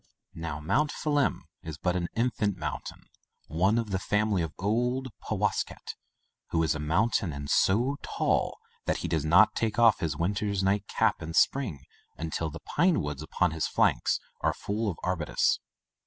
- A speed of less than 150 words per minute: No, average, 170 wpm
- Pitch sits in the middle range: No, very low, 95 Hz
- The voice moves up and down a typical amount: No, wide, 5.7 semitones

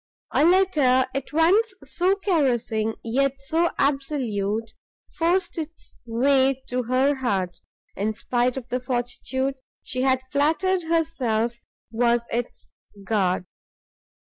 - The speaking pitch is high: Yes, very high, 260 Hz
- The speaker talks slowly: Yes, slow, 115 wpm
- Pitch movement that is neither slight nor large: Yes, average, 5.0 semitones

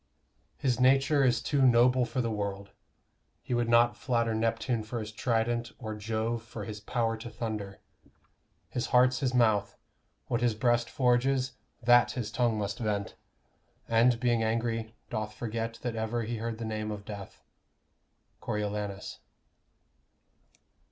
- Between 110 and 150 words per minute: Yes, average, 145 wpm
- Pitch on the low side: Yes, low, 115 Hz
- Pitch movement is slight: Yes, narrow, 2.1 semitones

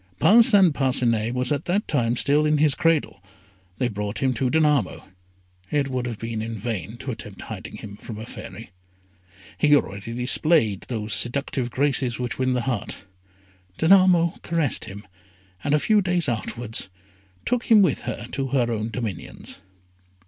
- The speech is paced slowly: No, average, 160 wpm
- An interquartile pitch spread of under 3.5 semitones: No, average, 4.9 semitones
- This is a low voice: Yes, low, 125 Hz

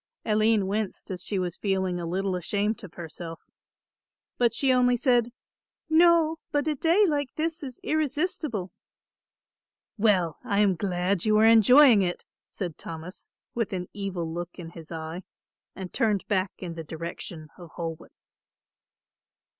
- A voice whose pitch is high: Yes, high, 200 Hz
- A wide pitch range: Yes, wide, 5.8 semitones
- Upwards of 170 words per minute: No, average, 145 wpm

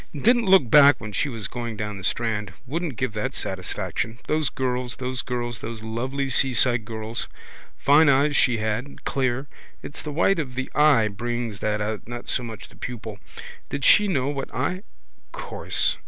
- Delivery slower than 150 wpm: No, average, 175 wpm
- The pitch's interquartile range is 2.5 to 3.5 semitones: No, average, 4.0 semitones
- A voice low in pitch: Yes, low, 125 Hz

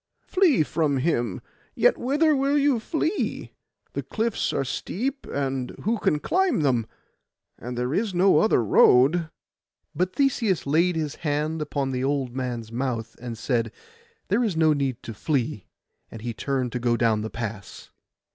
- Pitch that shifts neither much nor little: No, wide, 8.2 semitones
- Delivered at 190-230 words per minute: No, average, 160 wpm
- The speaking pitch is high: No, medium, 145 Hz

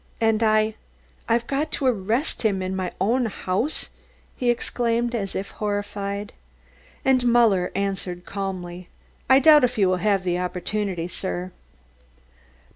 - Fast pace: No, slow, 135 wpm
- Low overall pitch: No, high, 205 Hz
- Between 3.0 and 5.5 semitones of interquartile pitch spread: Yes, average, 4.1 semitones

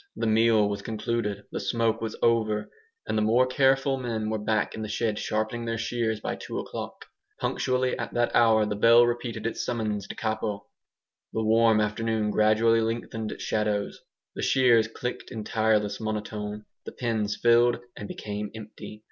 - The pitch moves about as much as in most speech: No, narrow, 1.6 semitones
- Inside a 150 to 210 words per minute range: Yes, average, 170 wpm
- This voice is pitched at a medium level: No, low, 110 Hz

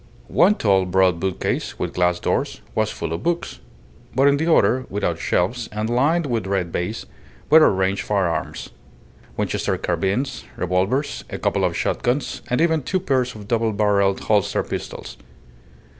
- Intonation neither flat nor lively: No, wide, 5.8 semitones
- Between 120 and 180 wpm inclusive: Yes, average, 160 wpm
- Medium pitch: No, low, 105 Hz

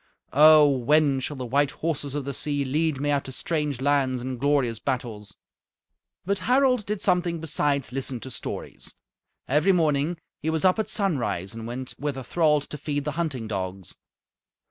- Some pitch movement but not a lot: Yes, average, 3.3 semitones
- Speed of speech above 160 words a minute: Yes, average, 175 wpm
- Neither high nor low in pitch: Yes, medium, 145 Hz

